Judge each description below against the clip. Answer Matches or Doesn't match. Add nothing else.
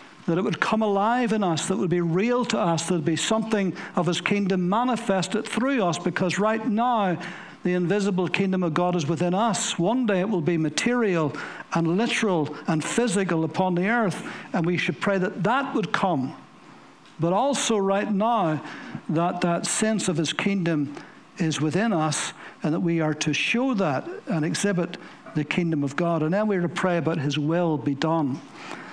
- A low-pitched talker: Doesn't match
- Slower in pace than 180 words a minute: Doesn't match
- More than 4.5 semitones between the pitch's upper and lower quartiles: Doesn't match